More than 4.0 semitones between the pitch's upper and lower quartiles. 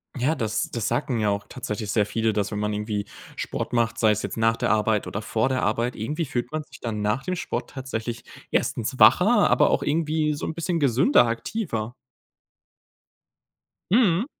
Yes: average, 5.2 semitones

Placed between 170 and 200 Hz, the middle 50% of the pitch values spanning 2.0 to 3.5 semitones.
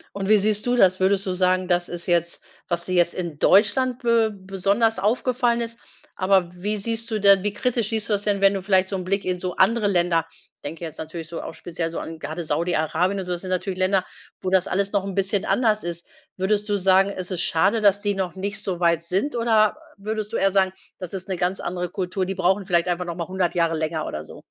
Yes: high, 190 Hz; narrow, 2.5 semitones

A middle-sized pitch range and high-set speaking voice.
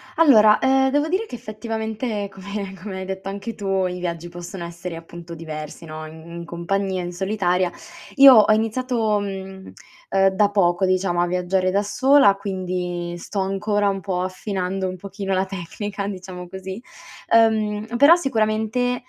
Yes: average, 3.0 semitones; high, 195 Hz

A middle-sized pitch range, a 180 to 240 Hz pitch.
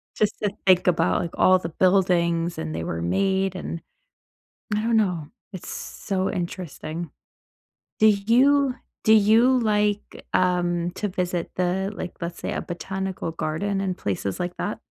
Yes: average, 3.1 semitones; medium, 185 Hz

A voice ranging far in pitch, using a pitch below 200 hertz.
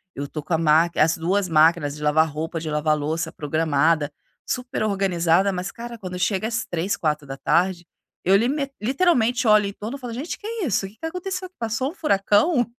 Yes: wide, 6.9 semitones; high, 190 Hz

